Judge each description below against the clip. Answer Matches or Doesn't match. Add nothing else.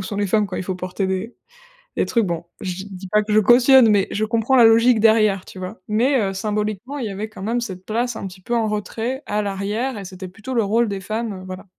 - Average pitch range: Matches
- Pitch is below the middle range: Doesn't match